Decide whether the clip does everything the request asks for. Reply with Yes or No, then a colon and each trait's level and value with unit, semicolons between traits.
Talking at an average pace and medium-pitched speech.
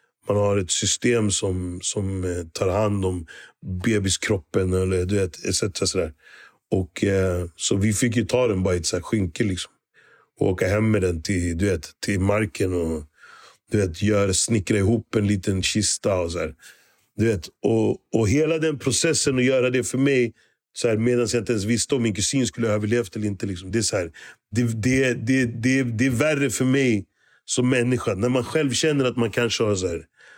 No: average, 180 wpm; low, 110 Hz